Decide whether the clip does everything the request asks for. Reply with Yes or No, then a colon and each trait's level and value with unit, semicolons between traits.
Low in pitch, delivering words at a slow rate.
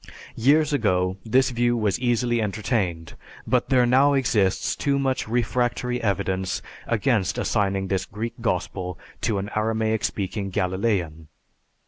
Yes: low, 110 Hz; slow, 125 wpm